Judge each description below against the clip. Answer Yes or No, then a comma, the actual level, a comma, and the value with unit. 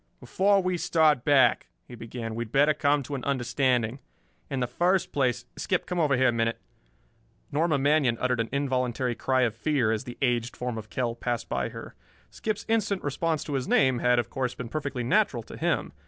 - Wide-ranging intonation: No, average, 3.5 semitones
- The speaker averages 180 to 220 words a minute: Yes, average, 200 wpm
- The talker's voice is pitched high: No, low, 130 Hz